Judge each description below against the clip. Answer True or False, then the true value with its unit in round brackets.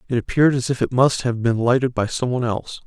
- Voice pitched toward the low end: True (125 Hz)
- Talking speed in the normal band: False (270 wpm)